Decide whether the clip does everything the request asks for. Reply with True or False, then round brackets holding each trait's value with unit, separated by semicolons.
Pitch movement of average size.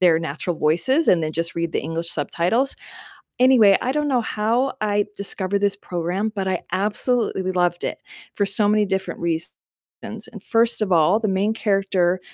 True (3.8 semitones)